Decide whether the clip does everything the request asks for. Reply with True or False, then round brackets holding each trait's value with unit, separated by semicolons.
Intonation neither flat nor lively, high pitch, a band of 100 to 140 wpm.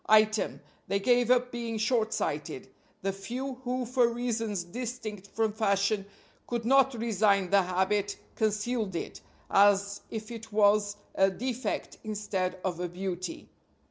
True (3.2 semitones; 215 Hz; 135 wpm)